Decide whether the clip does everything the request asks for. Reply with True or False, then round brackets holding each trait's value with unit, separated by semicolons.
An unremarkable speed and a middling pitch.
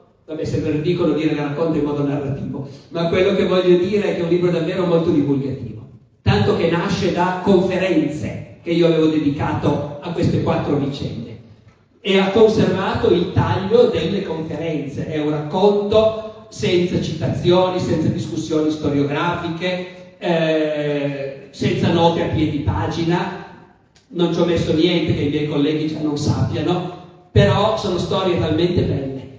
True (150 wpm; 165 Hz)